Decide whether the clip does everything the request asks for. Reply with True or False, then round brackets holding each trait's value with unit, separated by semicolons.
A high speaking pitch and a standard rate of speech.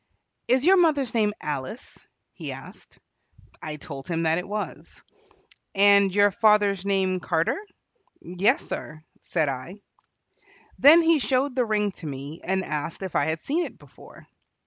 True (195 Hz; 150 wpm)